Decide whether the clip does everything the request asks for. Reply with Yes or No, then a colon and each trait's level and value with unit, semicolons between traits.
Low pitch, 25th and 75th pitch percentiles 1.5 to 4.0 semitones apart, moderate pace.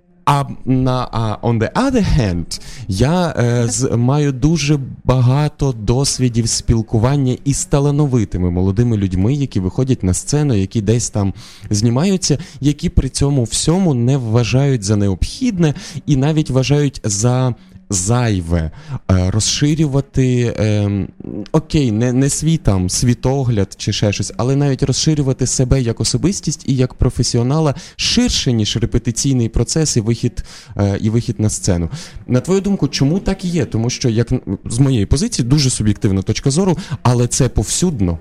No: low, 125 Hz; average, 4.7 semitones; average, 140 wpm